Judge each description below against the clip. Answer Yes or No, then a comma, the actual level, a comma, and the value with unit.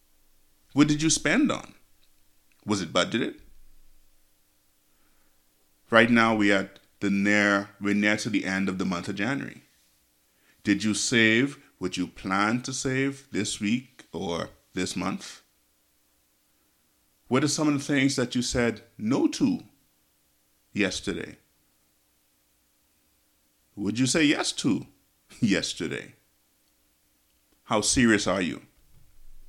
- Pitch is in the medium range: No, very low, 85 Hz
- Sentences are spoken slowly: Yes, slow, 120 wpm